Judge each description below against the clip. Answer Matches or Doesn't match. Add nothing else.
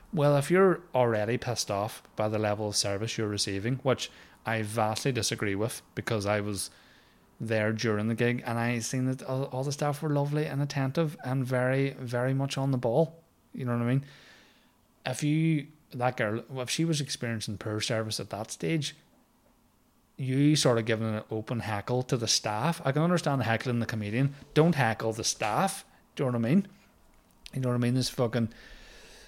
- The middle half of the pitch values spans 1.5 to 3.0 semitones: Doesn't match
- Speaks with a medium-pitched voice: Doesn't match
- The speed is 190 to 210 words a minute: Matches